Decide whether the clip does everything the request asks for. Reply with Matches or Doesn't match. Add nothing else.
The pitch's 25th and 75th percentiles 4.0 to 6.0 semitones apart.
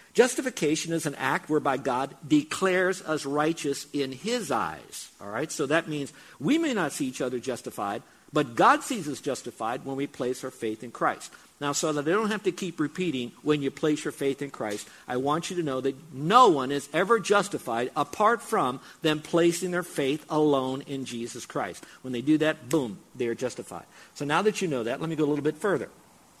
Matches